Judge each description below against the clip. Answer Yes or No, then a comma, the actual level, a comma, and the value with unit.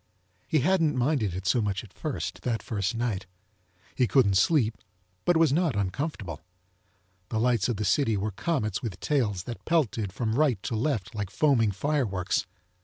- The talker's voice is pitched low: Yes, low, 115 Hz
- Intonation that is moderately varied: No, wide, 6.0 semitones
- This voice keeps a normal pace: Yes, average, 175 wpm